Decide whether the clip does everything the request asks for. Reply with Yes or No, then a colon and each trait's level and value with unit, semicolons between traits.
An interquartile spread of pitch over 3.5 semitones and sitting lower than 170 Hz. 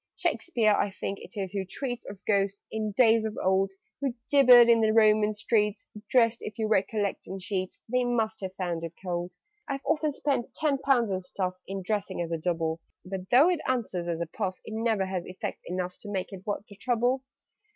No: average, 4.0 semitones; high, 210 Hz